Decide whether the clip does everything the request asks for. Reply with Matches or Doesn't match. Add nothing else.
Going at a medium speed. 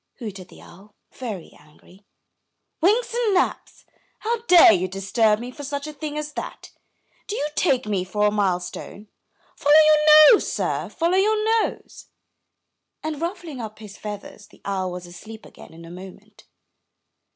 Matches